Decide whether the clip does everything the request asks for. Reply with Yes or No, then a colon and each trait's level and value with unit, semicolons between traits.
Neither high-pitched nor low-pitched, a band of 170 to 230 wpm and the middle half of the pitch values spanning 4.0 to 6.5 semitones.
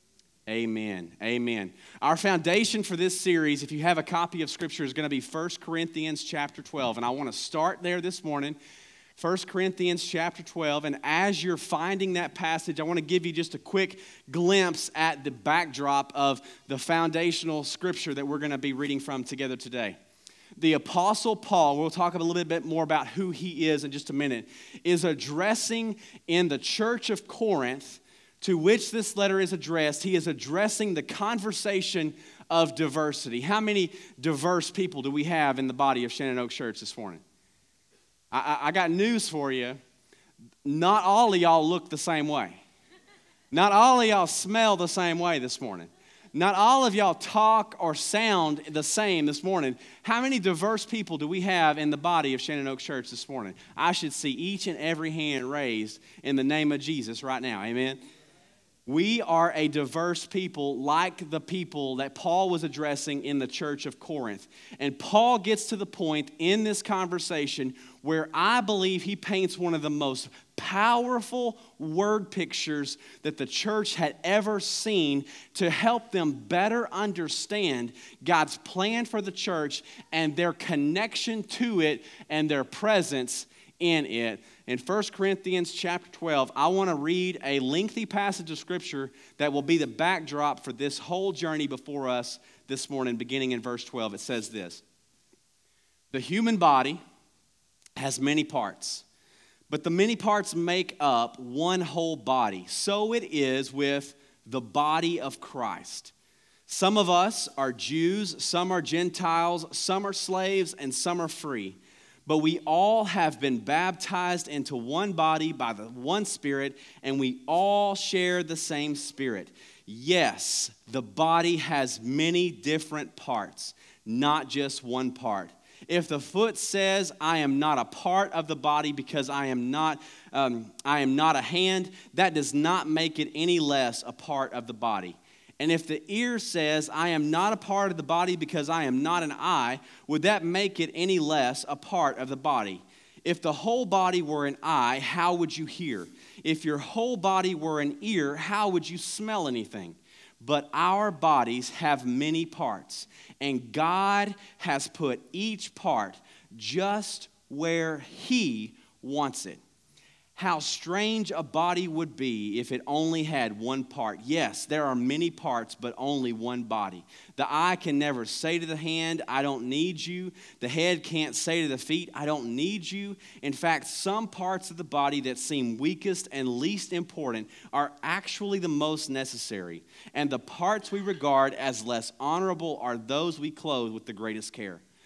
Yes: medium, 160 Hz; average, 175 wpm; average, 4.9 semitones